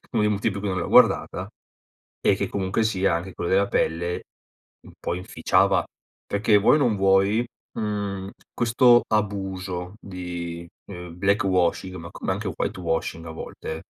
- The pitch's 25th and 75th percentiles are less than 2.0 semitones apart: No, narrow, 2.6 semitones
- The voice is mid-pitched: No, very low, 95 Hz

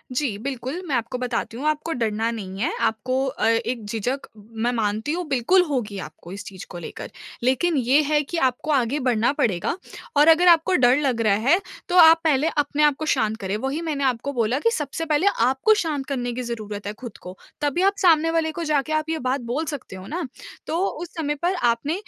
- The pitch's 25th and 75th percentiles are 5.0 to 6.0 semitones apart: Yes, average, 5.3 semitones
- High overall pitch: Yes, very high, 270 Hz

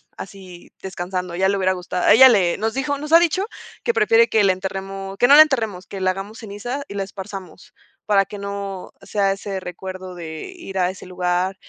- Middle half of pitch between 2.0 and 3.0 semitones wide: Yes, average, 2.7 semitones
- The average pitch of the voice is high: Yes, high, 195 Hz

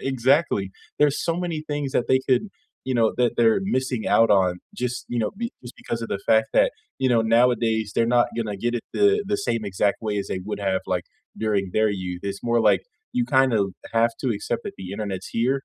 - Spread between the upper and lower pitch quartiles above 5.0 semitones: No, average, 3.6 semitones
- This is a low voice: Yes, low, 115 Hz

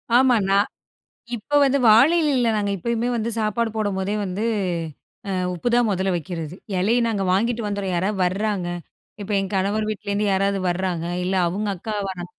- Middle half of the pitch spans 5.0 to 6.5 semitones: No, average, 3.0 semitones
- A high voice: Yes, high, 205 Hz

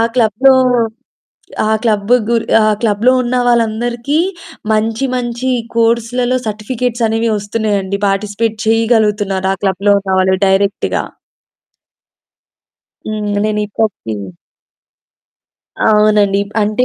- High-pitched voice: Yes, high, 215 Hz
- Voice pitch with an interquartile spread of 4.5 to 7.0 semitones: No, narrow, 2.5 semitones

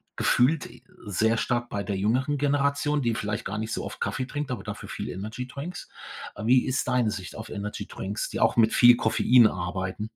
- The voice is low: Yes, low, 115 Hz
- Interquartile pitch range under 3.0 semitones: No, average, 3.7 semitones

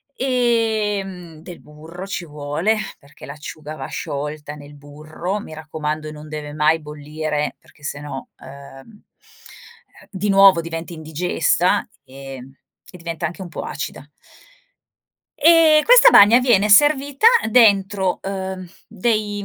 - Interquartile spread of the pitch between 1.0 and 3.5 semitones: No, wide, 5.4 semitones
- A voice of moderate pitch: Yes, medium, 170 Hz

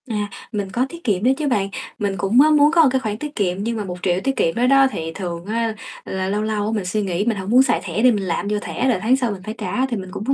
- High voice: Yes, high, 215 Hz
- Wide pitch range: No, average, 4.7 semitones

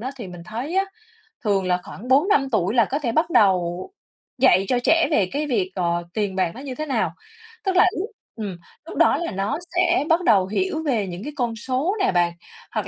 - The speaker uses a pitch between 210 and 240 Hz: Yes, high, 235 Hz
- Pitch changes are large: Yes, wide, 8.0 semitones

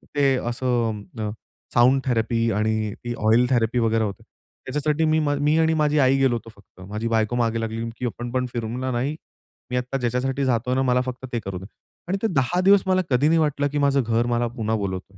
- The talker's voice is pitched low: Yes, low, 125 Hz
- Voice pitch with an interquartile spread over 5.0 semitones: No, average, 3.4 semitones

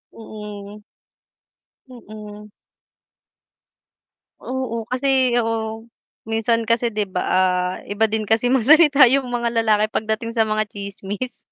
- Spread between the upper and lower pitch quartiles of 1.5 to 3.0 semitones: Yes, narrow, 2.4 semitones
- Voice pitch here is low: No, high, 220 Hz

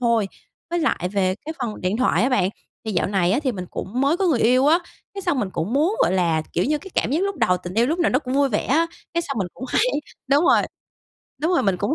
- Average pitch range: No, wide, 8.3 semitones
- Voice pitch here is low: No, very high, 255 Hz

